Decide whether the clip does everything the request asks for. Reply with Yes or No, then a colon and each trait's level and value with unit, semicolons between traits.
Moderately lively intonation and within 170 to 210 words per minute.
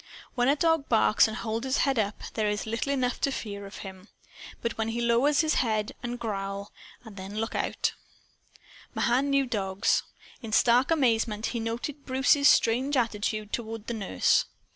Yes: average, 3.6 semitones; average, 175 wpm